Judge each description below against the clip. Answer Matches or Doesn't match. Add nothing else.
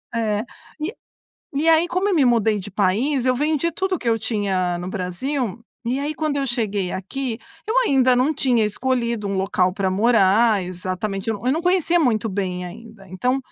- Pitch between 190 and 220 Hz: Doesn't match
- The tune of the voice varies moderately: Doesn't match